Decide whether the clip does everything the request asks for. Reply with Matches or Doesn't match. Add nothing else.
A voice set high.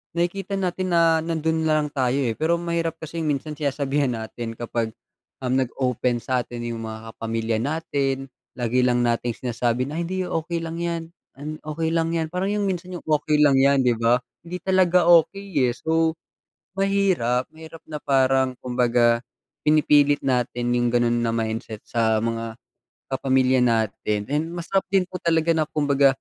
Doesn't match